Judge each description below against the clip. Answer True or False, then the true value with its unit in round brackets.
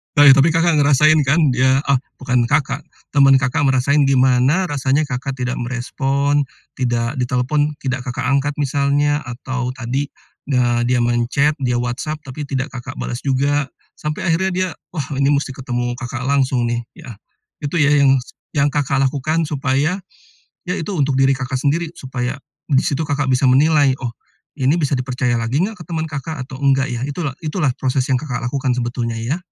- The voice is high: False (135 Hz)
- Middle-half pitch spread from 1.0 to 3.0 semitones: True (2.6 semitones)